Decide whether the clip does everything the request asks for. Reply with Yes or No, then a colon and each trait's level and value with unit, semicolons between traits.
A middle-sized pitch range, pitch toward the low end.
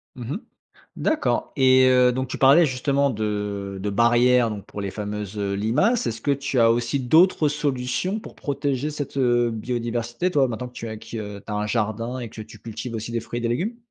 Yes: average, 3.6 semitones; low, 120 Hz